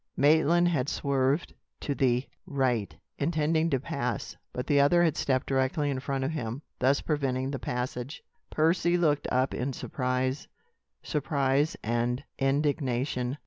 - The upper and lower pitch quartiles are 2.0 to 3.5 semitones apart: Yes, average, 2.8 semitones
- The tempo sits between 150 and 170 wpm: No, average, 140 wpm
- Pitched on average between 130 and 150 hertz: Yes, low, 135 Hz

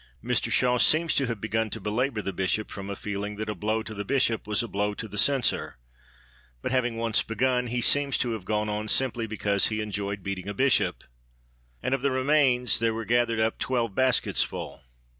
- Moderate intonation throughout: Yes, average, 3.1 semitones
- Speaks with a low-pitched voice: Yes, low, 115 Hz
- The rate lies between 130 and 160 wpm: No, fast, 205 wpm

